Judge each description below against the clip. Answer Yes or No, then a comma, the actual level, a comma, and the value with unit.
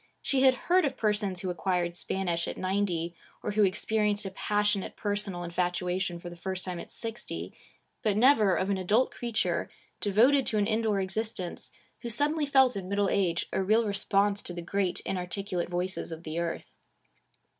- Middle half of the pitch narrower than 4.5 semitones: Yes, average, 3.3 semitones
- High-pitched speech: Yes, high, 200 Hz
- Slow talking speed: No, average, 175 wpm